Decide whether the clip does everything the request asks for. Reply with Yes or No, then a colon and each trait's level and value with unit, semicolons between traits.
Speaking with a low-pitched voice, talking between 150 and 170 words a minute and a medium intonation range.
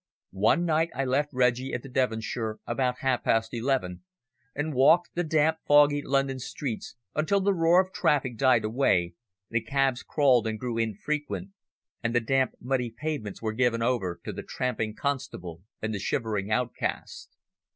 Yes: low, 125 Hz; average, 160 wpm; average, 4.4 semitones